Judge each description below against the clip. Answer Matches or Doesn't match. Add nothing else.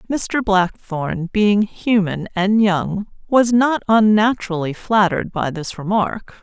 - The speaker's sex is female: Matches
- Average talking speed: Doesn't match